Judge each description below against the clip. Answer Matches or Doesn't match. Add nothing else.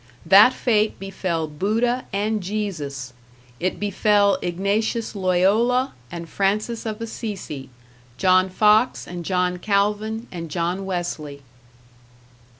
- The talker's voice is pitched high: Matches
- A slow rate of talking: Matches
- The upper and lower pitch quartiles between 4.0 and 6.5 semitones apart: Doesn't match